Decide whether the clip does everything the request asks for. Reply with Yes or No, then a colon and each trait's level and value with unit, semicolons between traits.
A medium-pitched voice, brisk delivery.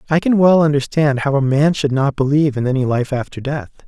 Yes: medium, 145 Hz; fast, 230 wpm